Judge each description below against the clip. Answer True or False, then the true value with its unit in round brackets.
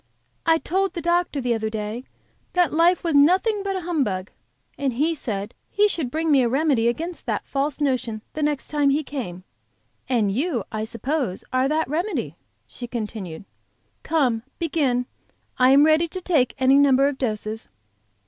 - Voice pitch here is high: True (275 Hz)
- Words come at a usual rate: True (170 wpm)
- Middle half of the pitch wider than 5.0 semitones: True (5.5 semitones)